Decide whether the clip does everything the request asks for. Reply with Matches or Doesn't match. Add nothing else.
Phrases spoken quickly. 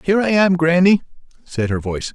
Doesn't match